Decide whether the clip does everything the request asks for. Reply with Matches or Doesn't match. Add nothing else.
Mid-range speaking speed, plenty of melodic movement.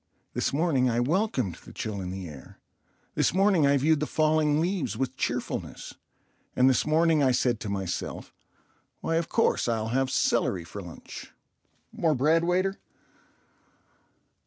Matches